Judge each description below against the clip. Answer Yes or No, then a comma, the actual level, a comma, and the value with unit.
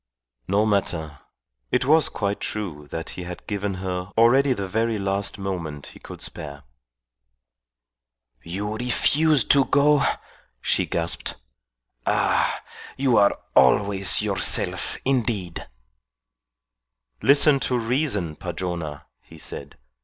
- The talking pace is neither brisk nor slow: No, slow, 110 wpm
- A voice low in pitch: Yes, low, 100 Hz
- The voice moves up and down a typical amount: No, wide, 5.7 semitones